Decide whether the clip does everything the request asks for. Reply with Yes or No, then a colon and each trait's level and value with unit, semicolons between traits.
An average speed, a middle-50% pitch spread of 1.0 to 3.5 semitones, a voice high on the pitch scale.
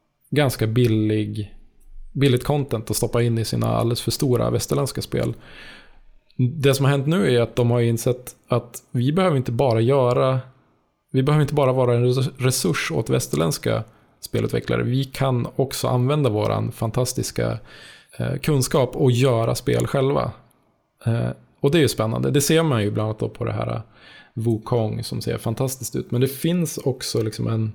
No: average, 165 wpm; average, 3.0 semitones; low, 125 Hz